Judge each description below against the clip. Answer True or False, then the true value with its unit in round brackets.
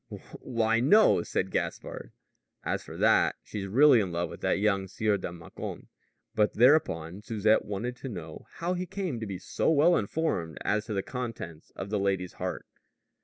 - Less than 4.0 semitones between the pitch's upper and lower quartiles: False (4.7 semitones)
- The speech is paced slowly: False (175 wpm)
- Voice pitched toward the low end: True (105 Hz)